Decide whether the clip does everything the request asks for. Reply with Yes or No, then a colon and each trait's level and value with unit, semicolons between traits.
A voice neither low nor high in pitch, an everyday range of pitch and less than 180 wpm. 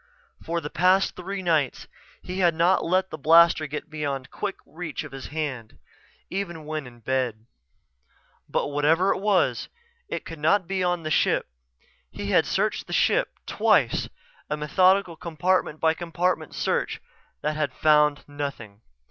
Yes: medium, 160 Hz; average, 3.5 semitones; average, 155 wpm